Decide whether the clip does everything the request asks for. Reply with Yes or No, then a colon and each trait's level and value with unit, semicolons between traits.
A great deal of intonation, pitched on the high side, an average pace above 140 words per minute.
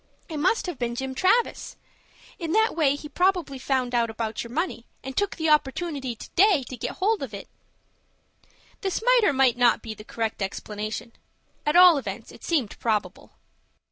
Yes: wide, 7.1 semitones; very high, 275 Hz; average, 180 wpm